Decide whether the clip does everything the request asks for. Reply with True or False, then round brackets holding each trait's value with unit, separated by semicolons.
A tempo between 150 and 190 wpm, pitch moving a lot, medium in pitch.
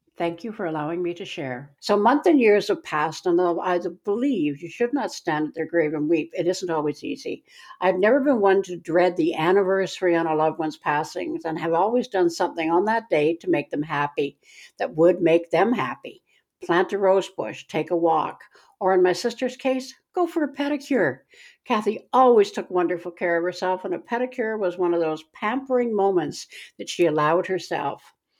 False (200 wpm; 5.9 semitones; 180 Hz)